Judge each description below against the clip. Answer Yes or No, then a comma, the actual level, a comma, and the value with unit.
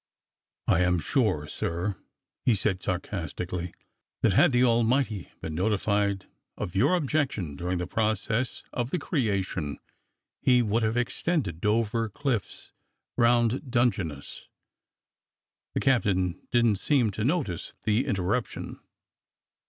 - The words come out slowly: Yes, slow, 115 wpm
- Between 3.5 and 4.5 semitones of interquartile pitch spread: No, average, 5.0 semitones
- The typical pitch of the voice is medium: No, low, 110 Hz